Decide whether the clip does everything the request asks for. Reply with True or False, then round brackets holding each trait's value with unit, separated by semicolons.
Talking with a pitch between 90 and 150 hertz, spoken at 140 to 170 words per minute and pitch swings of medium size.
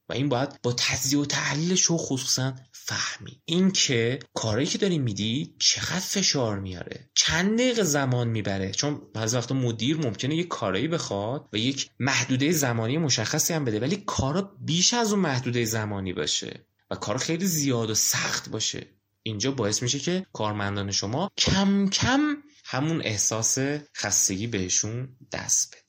False (135 Hz; 155 wpm; 6.5 semitones)